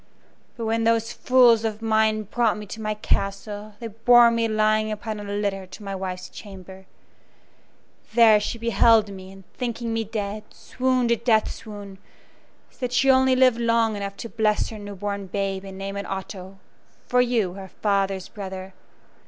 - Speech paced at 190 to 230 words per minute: No, average, 175 wpm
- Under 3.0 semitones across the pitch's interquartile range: Yes, narrow, 2.6 semitones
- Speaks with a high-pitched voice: Yes, high, 215 Hz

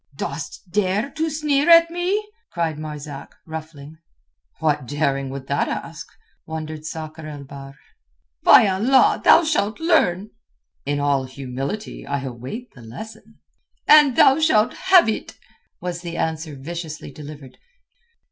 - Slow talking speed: Yes, slow, 130 wpm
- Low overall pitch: No, medium, 160 Hz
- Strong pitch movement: Yes, wide, 7.9 semitones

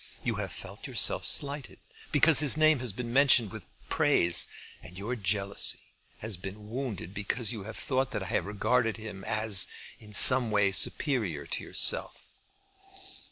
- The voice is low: Yes, low, 110 Hz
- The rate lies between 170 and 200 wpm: No, average, 160 wpm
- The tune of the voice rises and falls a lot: No, average, 4.3 semitones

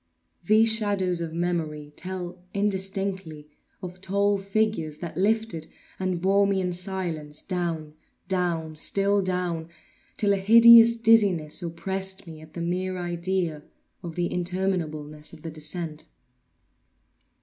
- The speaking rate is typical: No, slow, 115 wpm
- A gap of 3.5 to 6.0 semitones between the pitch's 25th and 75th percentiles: No, average, 3.1 semitones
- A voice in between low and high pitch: Yes, medium, 180 Hz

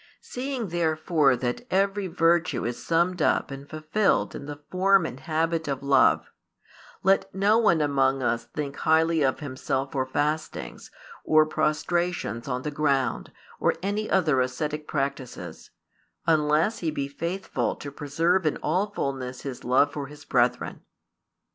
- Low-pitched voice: No, medium, 155 Hz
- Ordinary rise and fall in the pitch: Yes, average, 3.9 semitones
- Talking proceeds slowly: No, average, 145 wpm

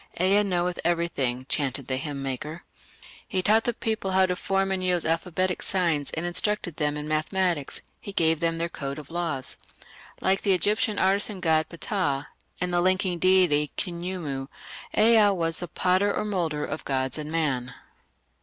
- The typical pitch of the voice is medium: Yes, medium, 175 Hz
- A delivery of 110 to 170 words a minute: Yes, average, 165 wpm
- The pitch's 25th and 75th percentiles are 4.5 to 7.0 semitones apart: No, average, 3.9 semitones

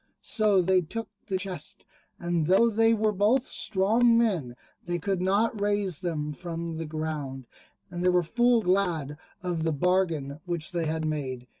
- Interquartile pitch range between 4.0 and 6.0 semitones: Yes, average, 4.4 semitones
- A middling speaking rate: Yes, average, 165 wpm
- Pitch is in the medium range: Yes, medium, 180 Hz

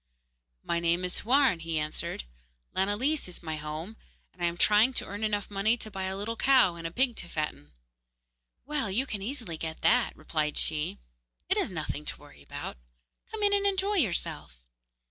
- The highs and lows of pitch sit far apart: Yes, wide, 6.8 semitones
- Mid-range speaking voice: No, high, 195 Hz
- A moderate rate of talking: Yes, average, 185 wpm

